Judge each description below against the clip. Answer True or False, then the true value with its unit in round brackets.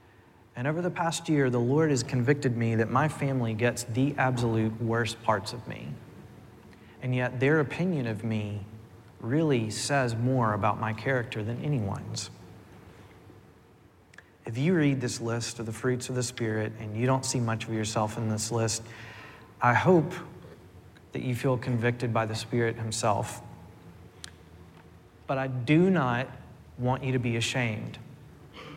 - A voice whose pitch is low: True (120 Hz)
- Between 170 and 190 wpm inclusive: False (155 wpm)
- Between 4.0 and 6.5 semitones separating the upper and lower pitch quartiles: False (3.0 semitones)